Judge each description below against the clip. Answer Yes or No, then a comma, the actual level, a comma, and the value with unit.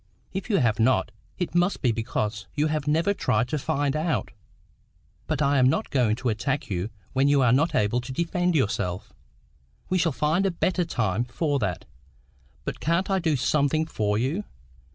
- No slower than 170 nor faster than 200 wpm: Yes, average, 180 wpm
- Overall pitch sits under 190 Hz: Yes, medium, 140 Hz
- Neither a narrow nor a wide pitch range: No, wide, 5.9 semitones